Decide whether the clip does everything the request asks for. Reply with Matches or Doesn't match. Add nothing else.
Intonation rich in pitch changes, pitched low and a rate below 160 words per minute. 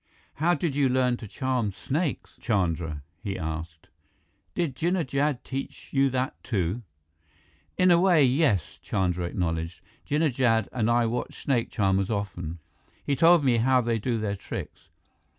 Matches